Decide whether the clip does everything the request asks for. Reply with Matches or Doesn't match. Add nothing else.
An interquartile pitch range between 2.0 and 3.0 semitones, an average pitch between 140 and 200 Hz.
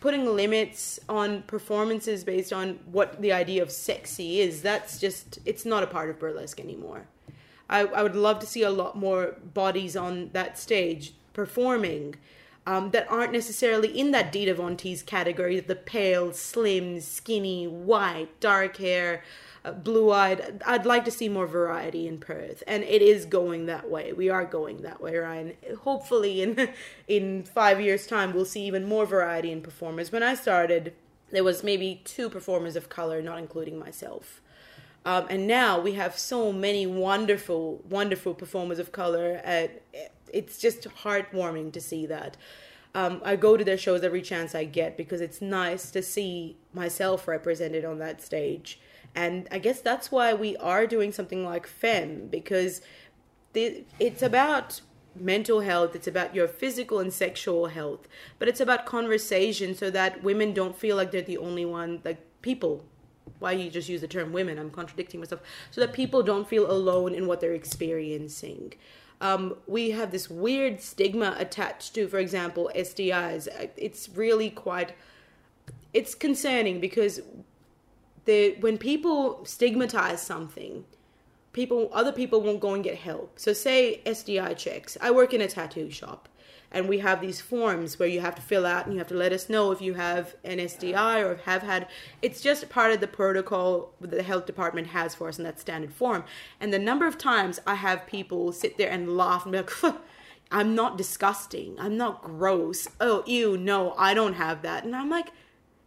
Doesn't match